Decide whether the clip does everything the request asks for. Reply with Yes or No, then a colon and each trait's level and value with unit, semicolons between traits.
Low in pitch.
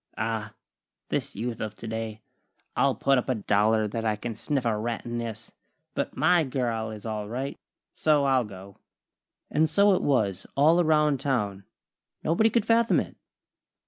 Yes: low, 115 Hz